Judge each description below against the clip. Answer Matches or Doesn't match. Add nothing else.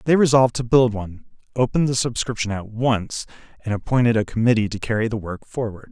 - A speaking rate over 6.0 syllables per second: Matches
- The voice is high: Doesn't match